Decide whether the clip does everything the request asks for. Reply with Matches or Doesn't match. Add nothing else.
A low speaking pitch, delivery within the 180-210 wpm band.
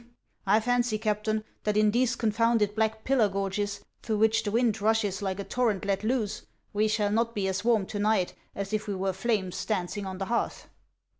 Doesn't match